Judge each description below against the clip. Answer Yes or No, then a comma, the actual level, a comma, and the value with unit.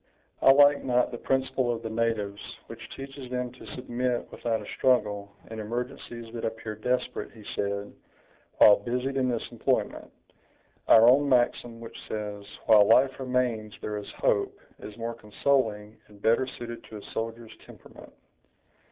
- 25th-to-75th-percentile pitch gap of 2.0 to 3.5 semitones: Yes, average, 2.8 semitones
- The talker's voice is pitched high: No, low, 115 Hz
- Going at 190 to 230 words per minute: No, average, 155 wpm